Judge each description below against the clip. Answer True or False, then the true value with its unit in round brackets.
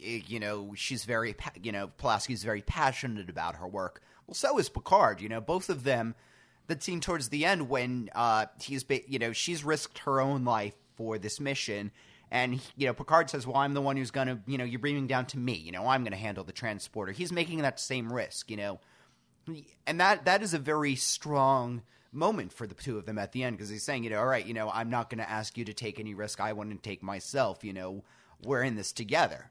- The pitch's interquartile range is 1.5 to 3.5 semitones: False (4.5 semitones)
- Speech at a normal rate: False (245 wpm)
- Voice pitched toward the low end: True (120 Hz)